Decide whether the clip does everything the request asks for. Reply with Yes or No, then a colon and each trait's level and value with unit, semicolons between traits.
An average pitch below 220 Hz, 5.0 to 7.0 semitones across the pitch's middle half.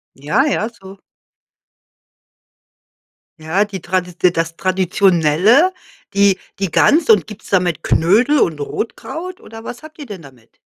Yes: high, 190 Hz; wide, 5.4 semitones